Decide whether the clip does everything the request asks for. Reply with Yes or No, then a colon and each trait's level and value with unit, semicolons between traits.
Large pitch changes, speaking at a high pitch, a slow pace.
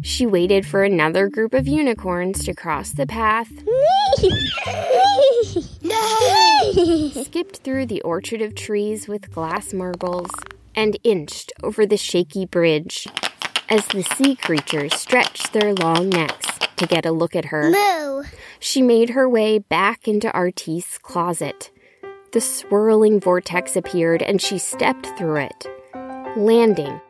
Yes: wide, 6.8 semitones; high, 210 Hz; slow, 130 wpm